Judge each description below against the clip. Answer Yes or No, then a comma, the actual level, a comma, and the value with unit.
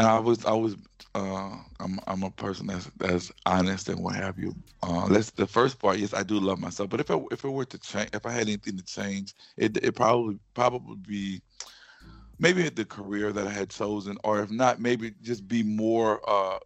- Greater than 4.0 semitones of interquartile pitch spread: No, average, 2.8 semitones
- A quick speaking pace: Yes, fast, 220 wpm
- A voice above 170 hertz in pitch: No, low, 105 Hz